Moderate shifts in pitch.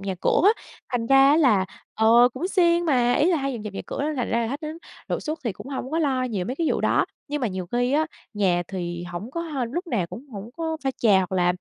No: wide, 6.9 semitones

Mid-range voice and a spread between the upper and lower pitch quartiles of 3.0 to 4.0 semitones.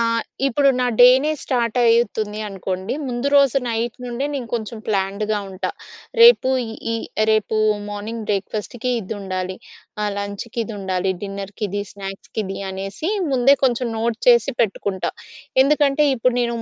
No: high, 220 Hz; average, 3.7 semitones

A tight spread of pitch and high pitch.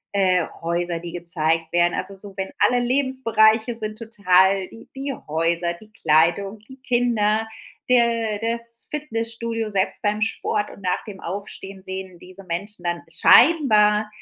No: average, 4.1 semitones; high, 205 Hz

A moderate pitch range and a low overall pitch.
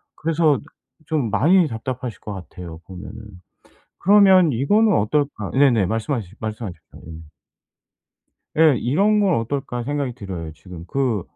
No: wide, 7.2 semitones; low, 125 Hz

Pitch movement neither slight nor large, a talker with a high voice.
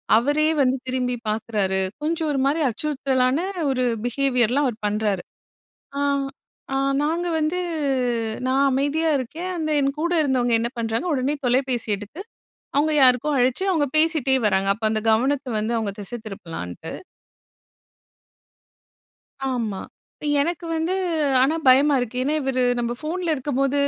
Yes: average, 4.4 semitones; very high, 260 Hz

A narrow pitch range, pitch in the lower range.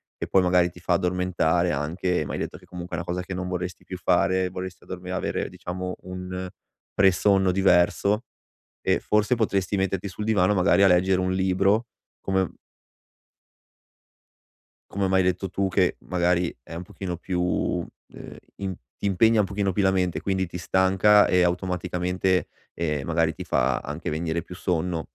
Yes: narrow, 1.4 semitones; very low, 90 Hz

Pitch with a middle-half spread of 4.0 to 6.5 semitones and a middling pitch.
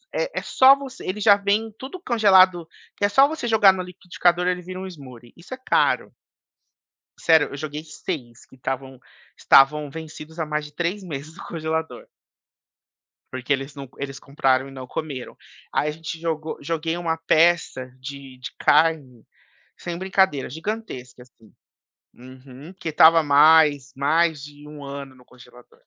Yes: average, 4.7 semitones; medium, 155 Hz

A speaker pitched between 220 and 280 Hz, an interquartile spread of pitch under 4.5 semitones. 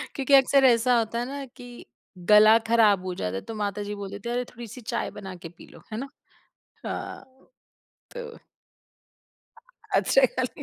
Yes: high, 230 Hz; average, 4.1 semitones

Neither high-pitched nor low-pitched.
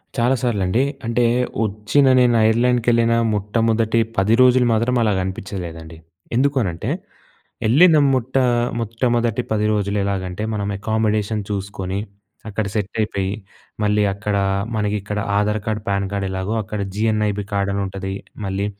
No: low, 105 Hz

